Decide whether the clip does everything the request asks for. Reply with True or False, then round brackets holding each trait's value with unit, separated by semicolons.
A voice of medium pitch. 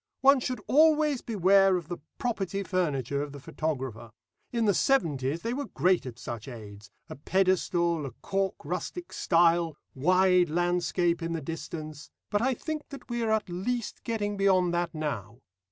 True (180 Hz)